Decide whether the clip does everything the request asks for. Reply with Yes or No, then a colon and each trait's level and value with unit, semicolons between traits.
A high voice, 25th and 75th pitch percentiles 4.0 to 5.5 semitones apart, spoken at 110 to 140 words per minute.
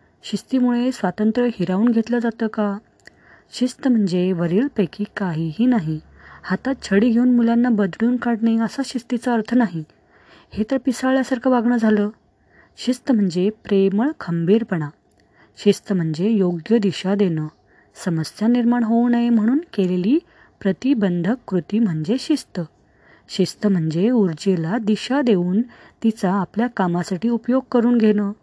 Yes: high, 215 Hz; average, 4.5 semitones; average, 120 wpm